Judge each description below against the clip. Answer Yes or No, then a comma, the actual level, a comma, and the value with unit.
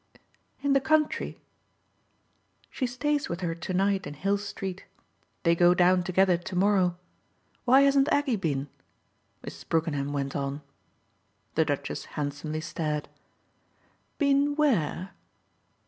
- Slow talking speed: Yes, slow, 120 wpm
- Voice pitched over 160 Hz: Yes, medium, 185 Hz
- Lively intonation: Yes, wide, 8.4 semitones